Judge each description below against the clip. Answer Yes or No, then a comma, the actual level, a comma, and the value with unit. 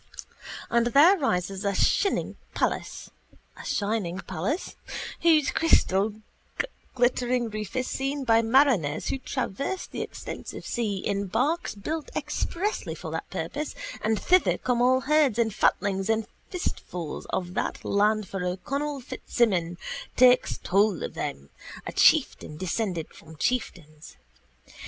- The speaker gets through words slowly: Yes, slow, 120 wpm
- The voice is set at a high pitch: Yes, high, 225 Hz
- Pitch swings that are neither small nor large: No, wide, 6.1 semitones